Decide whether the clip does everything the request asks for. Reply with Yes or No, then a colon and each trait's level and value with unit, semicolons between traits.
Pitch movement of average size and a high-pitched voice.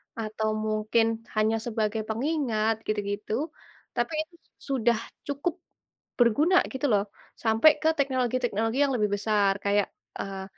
Yes: average, 3.6 semitones; high, 225 Hz